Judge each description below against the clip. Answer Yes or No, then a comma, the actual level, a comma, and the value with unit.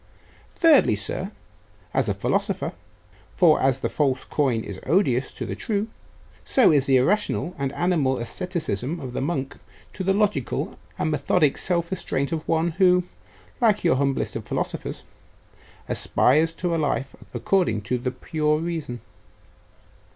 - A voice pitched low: No, medium, 155 Hz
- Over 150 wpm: No, average, 145 wpm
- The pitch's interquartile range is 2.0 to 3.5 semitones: No, average, 5.3 semitones